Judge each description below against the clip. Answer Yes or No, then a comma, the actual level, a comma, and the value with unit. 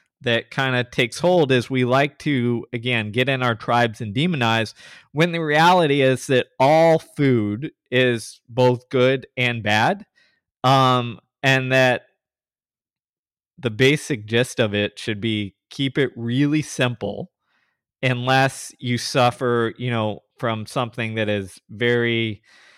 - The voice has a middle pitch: No, low, 125 Hz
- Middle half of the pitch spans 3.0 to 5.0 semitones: No, narrow, 2.6 semitones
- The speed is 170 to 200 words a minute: No, slow, 135 wpm